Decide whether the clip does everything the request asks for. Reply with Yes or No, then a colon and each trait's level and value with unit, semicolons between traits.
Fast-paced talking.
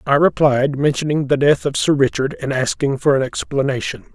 No: average, 190 wpm